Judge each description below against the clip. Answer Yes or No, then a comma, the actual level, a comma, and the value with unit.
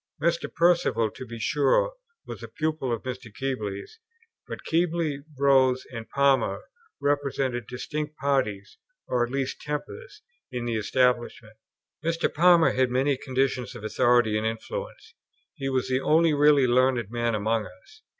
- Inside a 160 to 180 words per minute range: No, average, 145 wpm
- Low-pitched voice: Yes, low, 130 Hz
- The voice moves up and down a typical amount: Yes, average, 4.0 semitones